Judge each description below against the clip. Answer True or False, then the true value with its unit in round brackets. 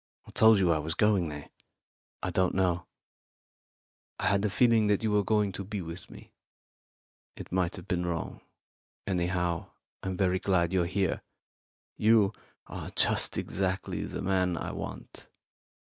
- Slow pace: False (155 wpm)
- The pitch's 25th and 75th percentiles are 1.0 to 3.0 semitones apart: True (2.6 semitones)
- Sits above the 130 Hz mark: False (95 Hz)